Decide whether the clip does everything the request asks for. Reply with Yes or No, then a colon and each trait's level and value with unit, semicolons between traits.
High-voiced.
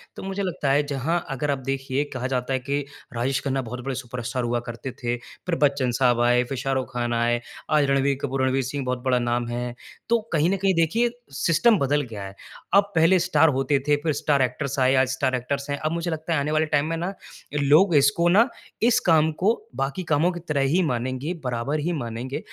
No: medium, 140 Hz